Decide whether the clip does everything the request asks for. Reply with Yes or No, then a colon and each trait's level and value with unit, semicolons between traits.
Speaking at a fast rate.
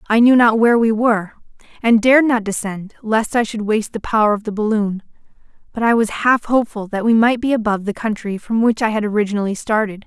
Yes: fast, 220 wpm